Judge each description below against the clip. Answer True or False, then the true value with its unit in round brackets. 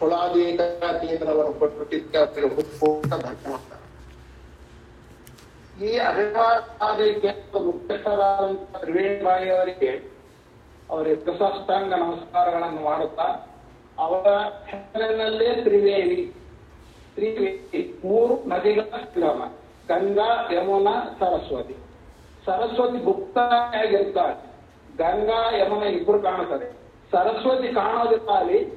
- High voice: True (200 Hz)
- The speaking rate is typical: False (50 wpm)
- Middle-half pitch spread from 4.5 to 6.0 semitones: True (5.2 semitones)